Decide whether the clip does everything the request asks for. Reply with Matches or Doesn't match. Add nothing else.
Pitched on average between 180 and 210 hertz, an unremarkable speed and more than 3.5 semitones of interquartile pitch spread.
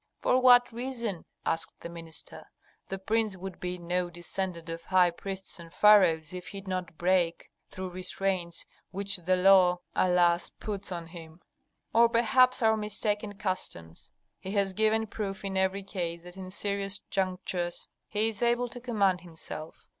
Doesn't match